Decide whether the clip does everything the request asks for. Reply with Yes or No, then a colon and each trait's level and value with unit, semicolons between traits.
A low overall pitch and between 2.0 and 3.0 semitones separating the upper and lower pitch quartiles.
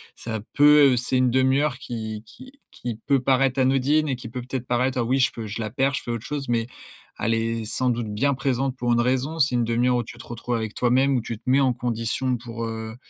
Yes: low, 125 Hz; narrow, 2.4 semitones